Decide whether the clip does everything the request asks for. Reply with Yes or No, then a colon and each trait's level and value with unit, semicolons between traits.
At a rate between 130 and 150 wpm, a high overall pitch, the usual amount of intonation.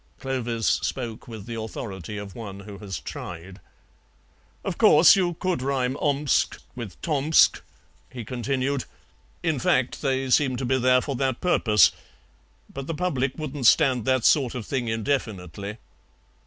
No: average, 145 wpm; low, 125 Hz; average, 3.9 semitones